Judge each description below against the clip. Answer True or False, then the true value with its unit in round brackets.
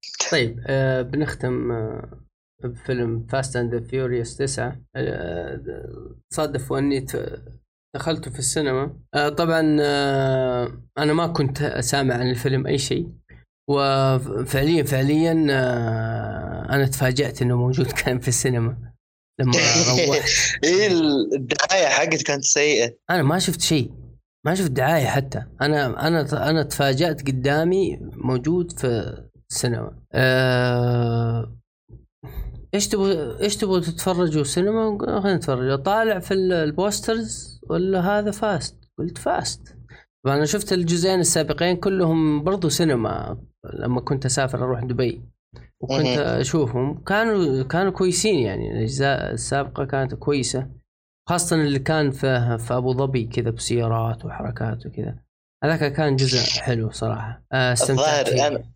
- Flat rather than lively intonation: False (4.5 semitones)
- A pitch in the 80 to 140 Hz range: True (135 Hz)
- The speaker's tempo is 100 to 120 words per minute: True (115 wpm)